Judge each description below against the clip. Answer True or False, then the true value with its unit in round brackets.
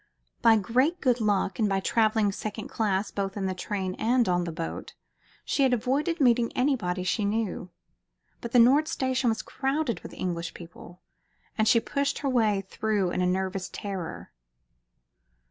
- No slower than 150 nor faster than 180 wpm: True (165 wpm)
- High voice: True (220 Hz)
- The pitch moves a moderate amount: True (4.7 semitones)